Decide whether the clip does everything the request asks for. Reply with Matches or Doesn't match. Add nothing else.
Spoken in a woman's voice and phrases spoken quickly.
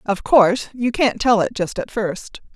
Matches